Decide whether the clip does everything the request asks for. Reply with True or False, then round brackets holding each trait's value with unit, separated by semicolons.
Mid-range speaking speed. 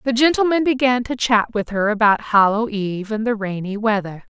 True (195 wpm)